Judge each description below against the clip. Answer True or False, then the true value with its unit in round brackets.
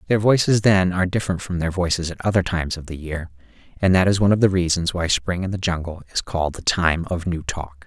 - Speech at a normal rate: False (250 wpm)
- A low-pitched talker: True (90 Hz)